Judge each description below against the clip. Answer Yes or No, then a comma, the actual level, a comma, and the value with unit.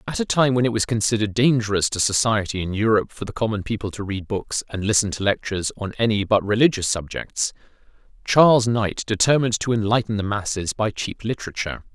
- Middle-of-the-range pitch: No, low, 110 Hz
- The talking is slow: No, average, 190 wpm